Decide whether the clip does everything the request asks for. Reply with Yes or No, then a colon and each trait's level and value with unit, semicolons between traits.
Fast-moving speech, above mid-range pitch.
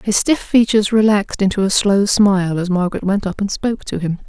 Yes: fast, 225 wpm; high, 200 Hz